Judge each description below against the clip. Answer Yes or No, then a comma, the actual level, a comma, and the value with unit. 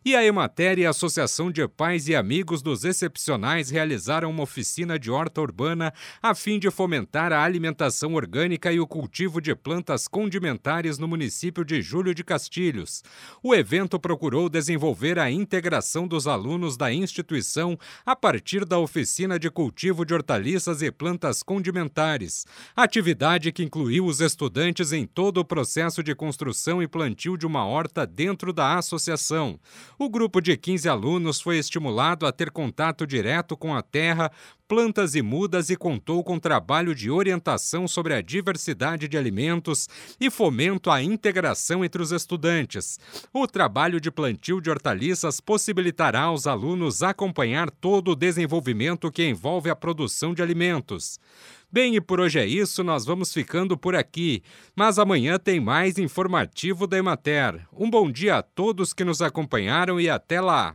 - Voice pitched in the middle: Yes, medium, 170 Hz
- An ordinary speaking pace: Yes, average, 160 wpm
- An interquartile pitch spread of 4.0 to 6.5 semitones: No, average, 2.8 semitones